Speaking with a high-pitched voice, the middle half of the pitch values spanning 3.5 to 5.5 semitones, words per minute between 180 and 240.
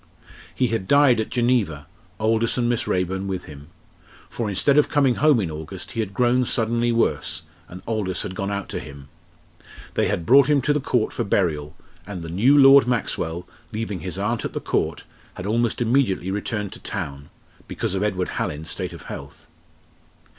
No: low, 105 Hz; average, 4.9 semitones; average, 185 wpm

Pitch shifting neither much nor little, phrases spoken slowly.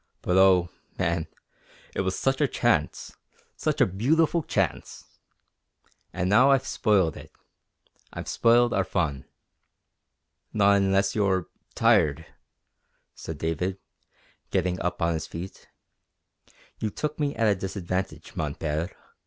Yes: average, 4.2 semitones; slow, 125 wpm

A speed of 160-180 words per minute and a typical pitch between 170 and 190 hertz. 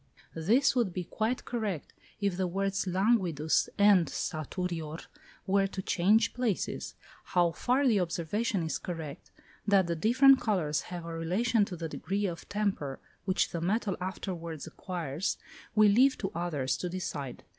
No: average, 150 wpm; medium, 185 Hz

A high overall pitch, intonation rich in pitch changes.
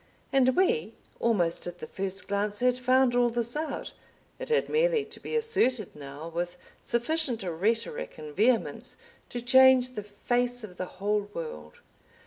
Yes: high, 235 Hz; wide, 5.9 semitones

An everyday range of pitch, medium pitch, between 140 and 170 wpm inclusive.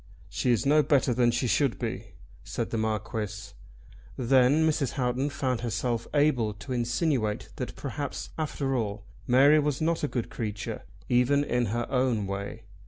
No: average, 4.1 semitones; low, 125 Hz; average, 160 wpm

